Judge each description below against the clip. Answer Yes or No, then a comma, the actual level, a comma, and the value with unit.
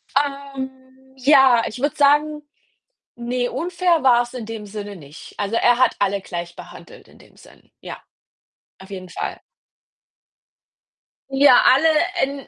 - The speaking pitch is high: Yes, very high, 260 Hz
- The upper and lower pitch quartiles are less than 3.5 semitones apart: No, average, 4.7 semitones